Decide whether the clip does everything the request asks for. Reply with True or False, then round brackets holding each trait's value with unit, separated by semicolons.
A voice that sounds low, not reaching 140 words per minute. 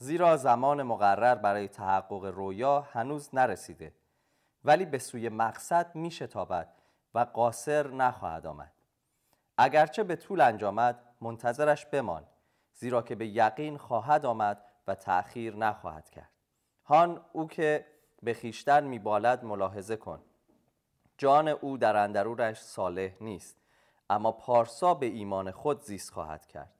True (120 Hz; 125 wpm)